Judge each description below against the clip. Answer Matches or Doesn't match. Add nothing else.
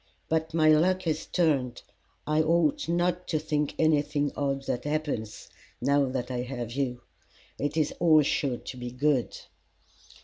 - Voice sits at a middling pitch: Matches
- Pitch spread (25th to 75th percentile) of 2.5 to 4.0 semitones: Matches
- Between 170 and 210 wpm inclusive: Doesn't match